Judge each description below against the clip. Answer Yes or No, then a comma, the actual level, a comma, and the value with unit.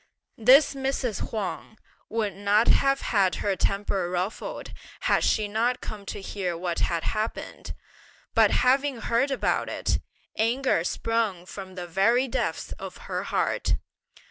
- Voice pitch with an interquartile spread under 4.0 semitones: No, average, 4.3 semitones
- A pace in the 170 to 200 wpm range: No, average, 140 wpm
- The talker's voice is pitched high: Yes, high, 215 Hz